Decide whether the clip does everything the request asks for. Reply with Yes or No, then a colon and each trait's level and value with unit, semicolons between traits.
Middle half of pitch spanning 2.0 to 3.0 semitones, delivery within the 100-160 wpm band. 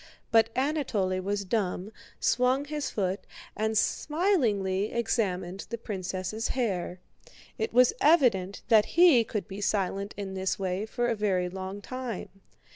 No: average, 4.1 semitones; slow, 135 wpm